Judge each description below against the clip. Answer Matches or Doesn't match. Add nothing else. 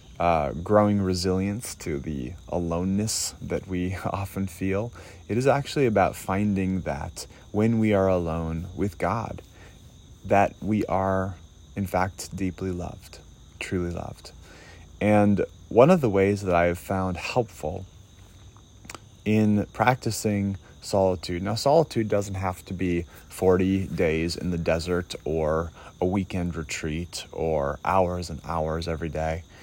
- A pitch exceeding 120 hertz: Doesn't match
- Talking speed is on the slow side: Matches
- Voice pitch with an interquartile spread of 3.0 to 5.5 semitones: Matches